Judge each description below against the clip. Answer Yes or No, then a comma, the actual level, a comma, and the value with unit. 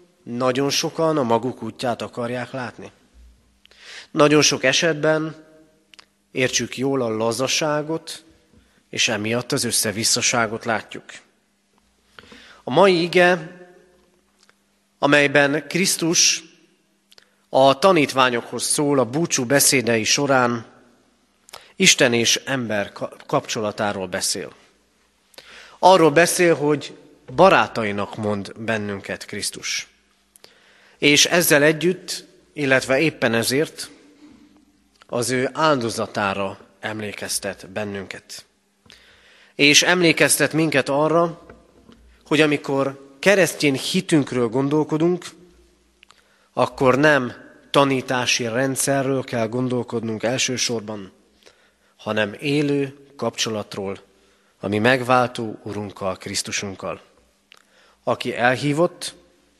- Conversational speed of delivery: No, slow, 80 wpm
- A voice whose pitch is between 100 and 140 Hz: Yes, low, 135 Hz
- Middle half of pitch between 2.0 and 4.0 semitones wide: No, wide, 5.4 semitones